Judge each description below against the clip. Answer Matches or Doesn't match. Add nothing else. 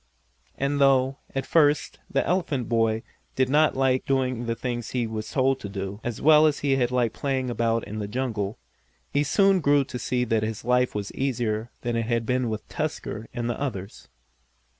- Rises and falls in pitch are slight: Doesn't match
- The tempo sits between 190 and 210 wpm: Matches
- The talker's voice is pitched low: Matches